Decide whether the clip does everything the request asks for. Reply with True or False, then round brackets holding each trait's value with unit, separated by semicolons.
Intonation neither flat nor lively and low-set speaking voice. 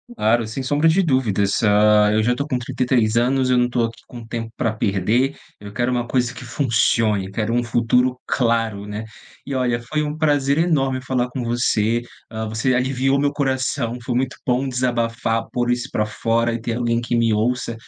False (2.3 semitones; 120 Hz)